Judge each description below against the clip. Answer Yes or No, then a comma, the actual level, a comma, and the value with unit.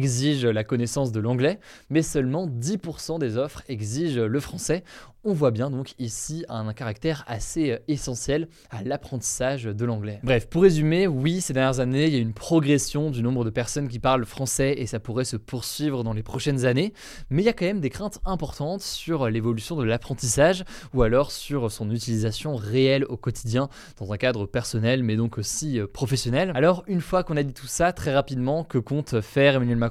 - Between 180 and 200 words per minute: Yes, average, 195 wpm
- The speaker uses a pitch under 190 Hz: Yes, low, 135 Hz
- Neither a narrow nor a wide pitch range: Yes, average, 4.4 semitones